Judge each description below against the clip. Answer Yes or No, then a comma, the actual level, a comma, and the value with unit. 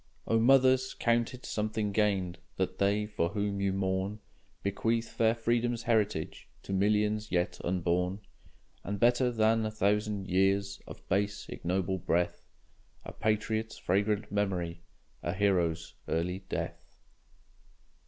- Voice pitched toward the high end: No, low, 100 Hz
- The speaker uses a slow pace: Yes, slow, 125 wpm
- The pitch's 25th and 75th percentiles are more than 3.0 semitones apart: No, average, 2.7 semitones